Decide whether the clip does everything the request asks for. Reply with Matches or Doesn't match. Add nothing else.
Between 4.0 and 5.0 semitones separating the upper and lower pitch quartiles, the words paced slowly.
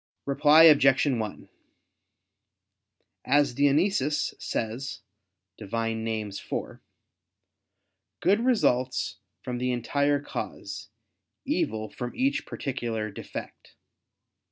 Matches